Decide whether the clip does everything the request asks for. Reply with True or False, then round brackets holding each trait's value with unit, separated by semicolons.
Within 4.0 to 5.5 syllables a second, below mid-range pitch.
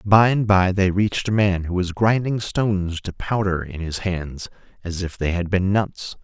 True (4.5 syllables/s; 95 Hz)